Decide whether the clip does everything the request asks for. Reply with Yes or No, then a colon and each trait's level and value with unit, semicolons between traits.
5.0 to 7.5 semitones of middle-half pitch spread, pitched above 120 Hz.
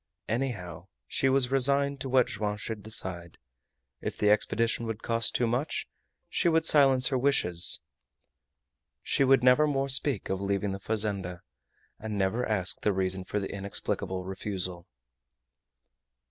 No: wide, 5.5 semitones; low, 110 Hz